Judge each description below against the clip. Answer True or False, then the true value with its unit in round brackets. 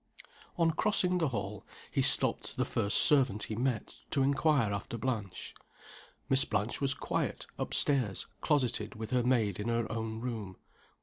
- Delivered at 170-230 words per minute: False (160 wpm)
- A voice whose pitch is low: True (120 Hz)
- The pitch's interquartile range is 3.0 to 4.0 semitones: False (4.4 semitones)